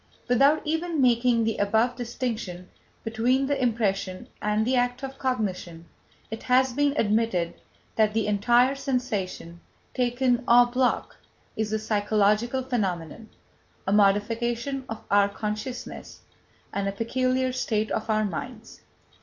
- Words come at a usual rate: No, slow, 130 wpm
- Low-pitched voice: No, high, 230 Hz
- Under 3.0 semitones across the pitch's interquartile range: No, average, 3.4 semitones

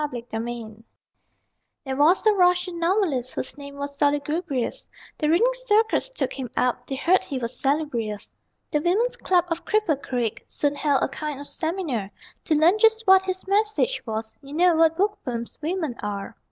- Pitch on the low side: No, very high, 300 Hz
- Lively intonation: Yes, wide, 6.5 semitones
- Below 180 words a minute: Yes, average, 170 wpm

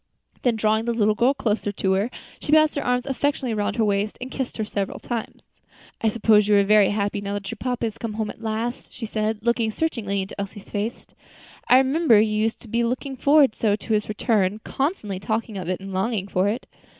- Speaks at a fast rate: Yes, fast, 220 wpm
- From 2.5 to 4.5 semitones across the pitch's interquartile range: Yes, average, 2.8 semitones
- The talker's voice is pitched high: Yes, high, 220 Hz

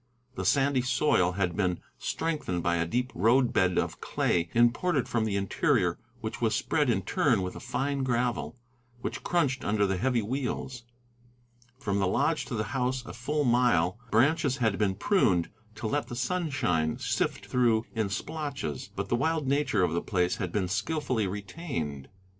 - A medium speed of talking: Yes, average, 170 wpm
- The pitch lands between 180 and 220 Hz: No, low, 120 Hz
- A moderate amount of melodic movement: No, wide, 6.0 semitones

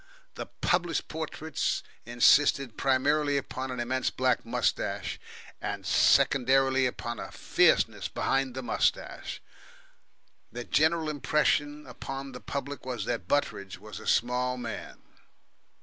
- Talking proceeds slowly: Yes, slow, 120 wpm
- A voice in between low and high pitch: No, low, 130 Hz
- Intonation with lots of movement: No, average, 2.8 semitones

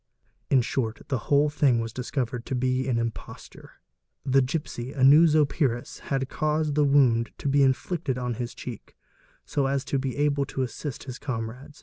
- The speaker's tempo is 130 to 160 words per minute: No, average, 180 wpm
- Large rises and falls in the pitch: No, narrow, 2.6 semitones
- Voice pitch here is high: No, low, 135 Hz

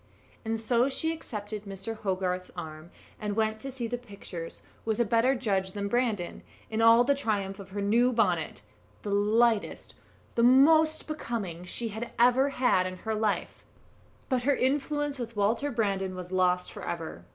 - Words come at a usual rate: Yes, average, 170 wpm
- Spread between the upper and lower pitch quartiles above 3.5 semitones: Yes, average, 4.0 semitones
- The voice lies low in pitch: No, high, 220 Hz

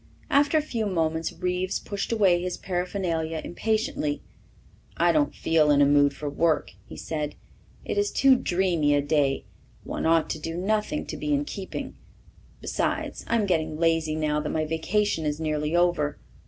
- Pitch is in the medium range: Yes, medium, 170 Hz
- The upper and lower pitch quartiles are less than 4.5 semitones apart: No, average, 5.2 semitones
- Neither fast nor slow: Yes, average, 170 wpm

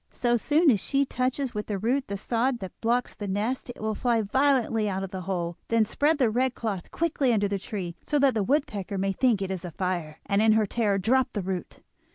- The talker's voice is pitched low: No, high, 220 Hz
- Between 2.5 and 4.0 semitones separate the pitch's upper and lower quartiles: No, average, 4.7 semitones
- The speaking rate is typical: No, fast, 235 wpm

